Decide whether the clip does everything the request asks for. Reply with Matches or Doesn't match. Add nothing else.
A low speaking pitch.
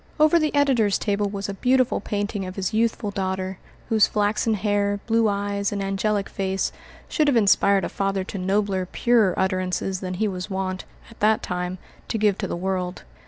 Doesn't match